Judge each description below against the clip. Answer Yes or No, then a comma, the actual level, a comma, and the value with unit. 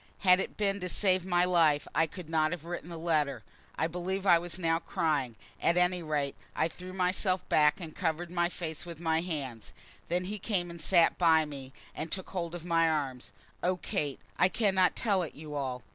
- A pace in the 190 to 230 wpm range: Yes, fast, 205 wpm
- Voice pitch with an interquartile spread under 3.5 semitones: Yes, average, 2.7 semitones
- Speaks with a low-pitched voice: No, medium, 170 Hz